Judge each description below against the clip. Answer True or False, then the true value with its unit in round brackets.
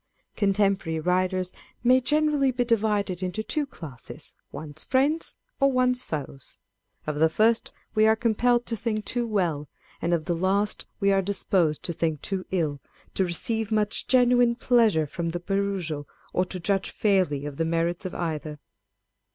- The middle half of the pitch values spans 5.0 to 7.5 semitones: True (5.6 semitones)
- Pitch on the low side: False (195 Hz)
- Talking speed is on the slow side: False (165 wpm)